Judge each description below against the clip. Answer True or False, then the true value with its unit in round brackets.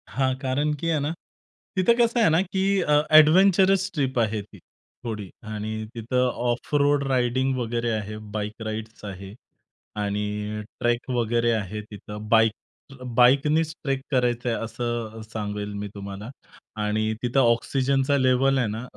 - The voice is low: True (120 Hz)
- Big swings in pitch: False (4.1 semitones)